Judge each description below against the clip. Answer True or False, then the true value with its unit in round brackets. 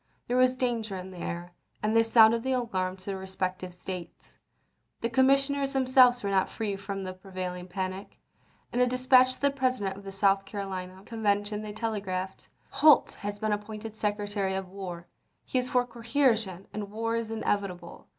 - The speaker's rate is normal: True (180 wpm)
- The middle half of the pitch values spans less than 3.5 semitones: False (3.9 semitones)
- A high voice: True (205 Hz)